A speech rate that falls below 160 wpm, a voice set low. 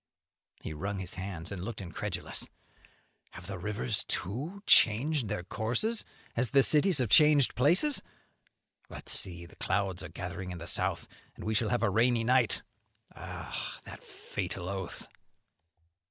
Yes: average, 150 wpm; low, 105 Hz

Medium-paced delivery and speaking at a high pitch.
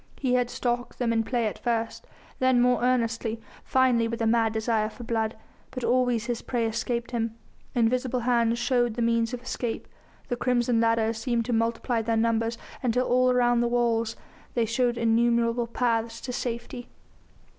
Yes: average, 170 wpm; high, 235 Hz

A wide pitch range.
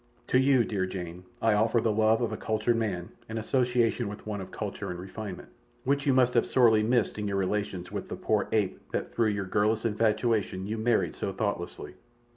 No: average, 2.7 semitones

